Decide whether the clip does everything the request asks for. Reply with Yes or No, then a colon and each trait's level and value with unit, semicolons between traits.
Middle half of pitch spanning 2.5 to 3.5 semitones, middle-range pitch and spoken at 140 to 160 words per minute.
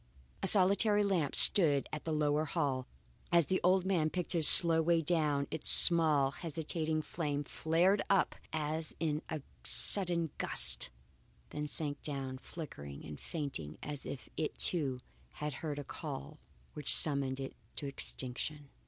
Yes: average, 2.9 semitones; medium, 155 Hz; average, 150 wpm